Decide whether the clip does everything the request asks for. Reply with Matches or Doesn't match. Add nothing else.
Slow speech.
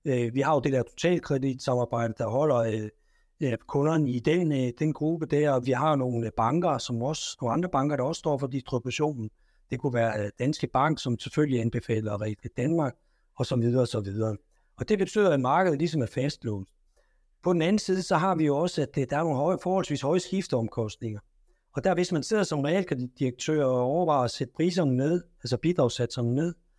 Doesn't match